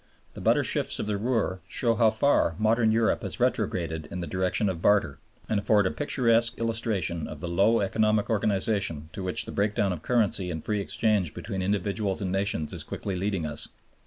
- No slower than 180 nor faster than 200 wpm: Yes, average, 190 wpm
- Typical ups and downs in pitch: Yes, average, 3.3 semitones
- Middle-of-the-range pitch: No, low, 100 Hz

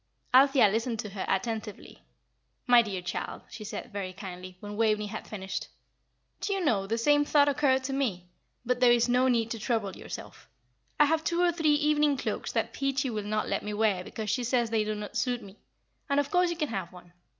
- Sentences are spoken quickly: Yes, fast, 215 wpm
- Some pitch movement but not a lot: Yes, average, 5.0 semitones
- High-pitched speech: Yes, high, 230 Hz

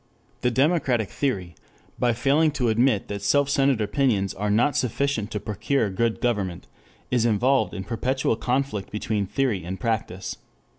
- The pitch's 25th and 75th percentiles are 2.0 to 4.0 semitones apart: No, average, 4.7 semitones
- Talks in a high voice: No, low, 115 Hz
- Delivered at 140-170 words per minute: Yes, average, 150 wpm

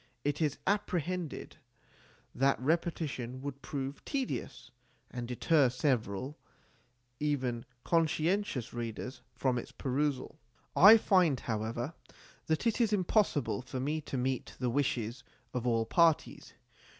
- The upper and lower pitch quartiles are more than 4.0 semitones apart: Yes, average, 4.8 semitones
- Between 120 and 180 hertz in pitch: Yes, medium, 140 Hz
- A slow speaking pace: Yes, slow, 120 wpm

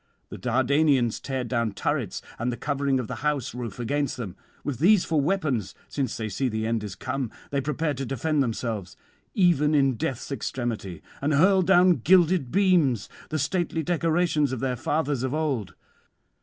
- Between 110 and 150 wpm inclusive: No, average, 170 wpm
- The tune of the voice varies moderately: Yes, average, 4.6 semitones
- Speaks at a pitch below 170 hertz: Yes, low, 135 Hz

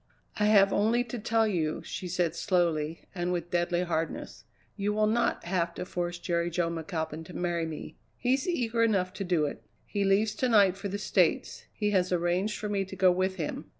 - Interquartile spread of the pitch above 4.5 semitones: No, average, 3.2 semitones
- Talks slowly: No, fast, 205 wpm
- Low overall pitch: No, medium, 185 Hz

